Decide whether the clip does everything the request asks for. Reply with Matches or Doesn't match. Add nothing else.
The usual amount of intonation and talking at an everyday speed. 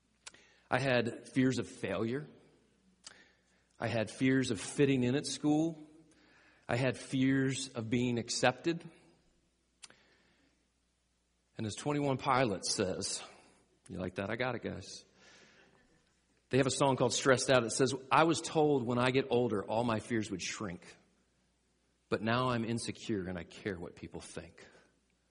Matches